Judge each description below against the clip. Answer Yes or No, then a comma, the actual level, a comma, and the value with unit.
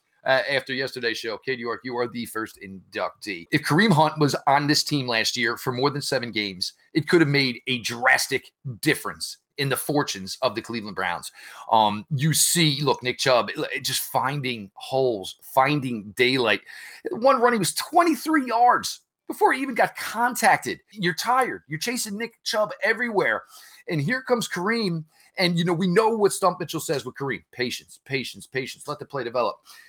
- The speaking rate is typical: Yes, average, 180 wpm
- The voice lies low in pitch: No, medium, 145 Hz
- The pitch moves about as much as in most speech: No, wide, 8.2 semitones